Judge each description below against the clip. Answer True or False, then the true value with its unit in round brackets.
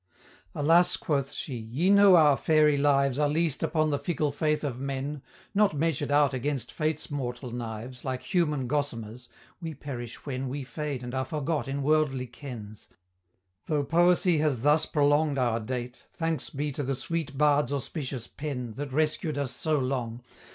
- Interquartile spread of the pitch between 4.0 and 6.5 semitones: False (3.1 semitones)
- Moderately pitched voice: True (145 Hz)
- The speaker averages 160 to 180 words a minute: True (165 wpm)